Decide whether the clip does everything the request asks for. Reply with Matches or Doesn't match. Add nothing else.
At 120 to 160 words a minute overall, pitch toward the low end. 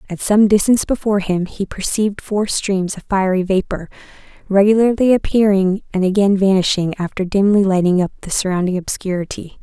Doesn't match